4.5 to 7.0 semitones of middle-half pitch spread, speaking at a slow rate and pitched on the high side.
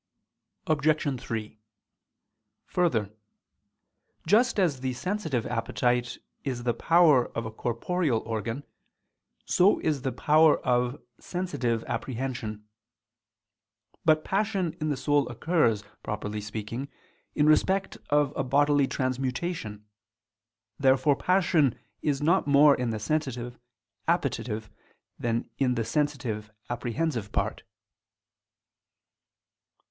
No: average, 4.9 semitones; slow, 100 wpm; low, 135 Hz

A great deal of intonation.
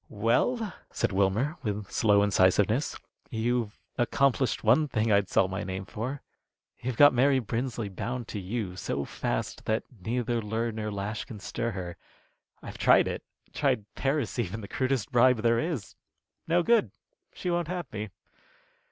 No: average, 4.1 semitones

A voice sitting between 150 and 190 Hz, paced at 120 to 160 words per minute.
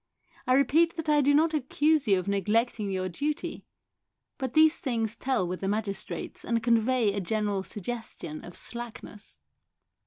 No: high, 230 Hz; average, 155 wpm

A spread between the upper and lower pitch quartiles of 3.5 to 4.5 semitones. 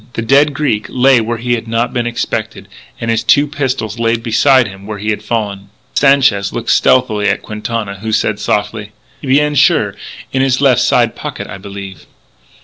Yes: average, 3.8 semitones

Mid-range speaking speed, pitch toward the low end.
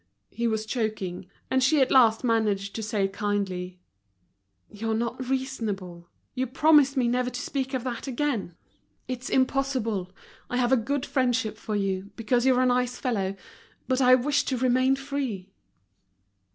No: average, 155 wpm; high, 245 Hz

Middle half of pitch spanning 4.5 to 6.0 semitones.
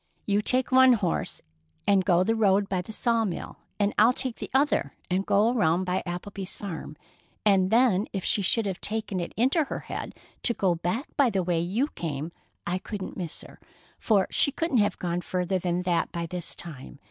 No: average, 4.1 semitones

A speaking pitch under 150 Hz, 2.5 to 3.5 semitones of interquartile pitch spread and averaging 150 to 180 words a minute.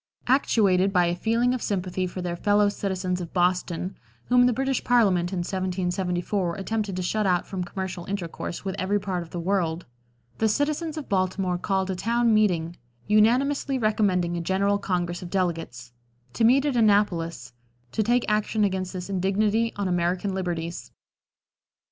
No: high, 190 Hz; average, 3.2 semitones; average, 160 wpm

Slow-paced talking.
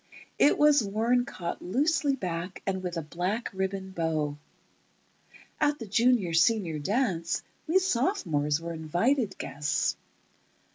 Yes: slow, 125 wpm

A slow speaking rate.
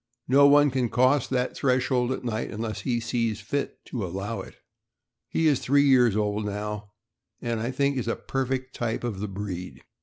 No: average, 185 wpm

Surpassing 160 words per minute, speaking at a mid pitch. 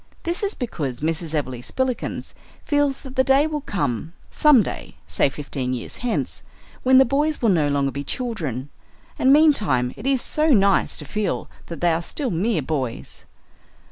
No: average, 170 wpm; high, 200 Hz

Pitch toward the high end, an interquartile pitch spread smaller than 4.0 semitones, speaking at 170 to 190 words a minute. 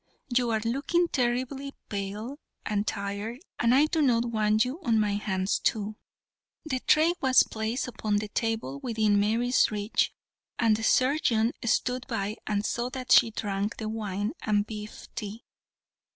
No: high, 225 Hz; average, 3.1 semitones; average, 155 wpm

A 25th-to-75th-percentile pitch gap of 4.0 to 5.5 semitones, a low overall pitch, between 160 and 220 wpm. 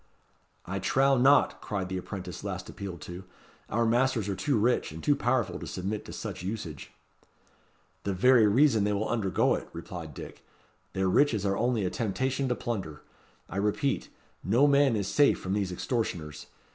Yes: average, 5.0 semitones; low, 105 Hz; average, 170 wpm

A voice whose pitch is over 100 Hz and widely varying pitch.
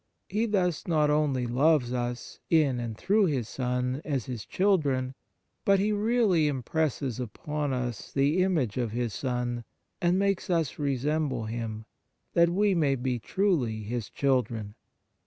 Yes: low, 135 Hz; wide, 5.7 semitones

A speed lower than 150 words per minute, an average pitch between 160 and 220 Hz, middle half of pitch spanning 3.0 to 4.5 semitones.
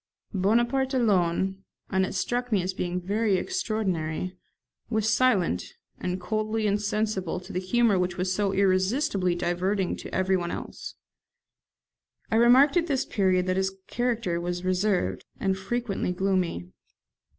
Yes: slow, 135 wpm; high, 190 Hz; average, 3.3 semitones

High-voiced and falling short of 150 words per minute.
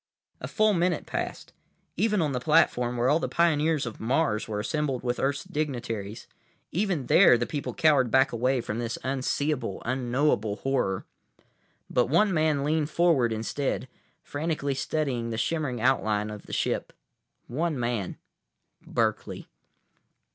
No: low, 135 Hz; average, 140 wpm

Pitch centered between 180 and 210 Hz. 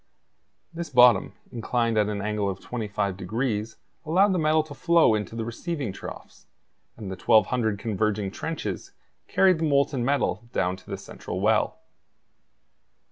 No: low, 115 Hz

